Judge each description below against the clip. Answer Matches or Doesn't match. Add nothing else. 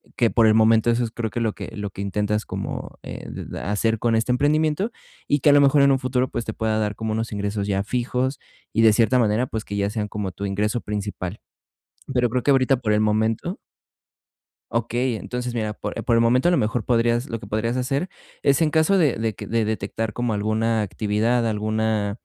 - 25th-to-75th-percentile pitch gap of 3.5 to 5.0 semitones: Doesn't match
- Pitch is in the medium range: Doesn't match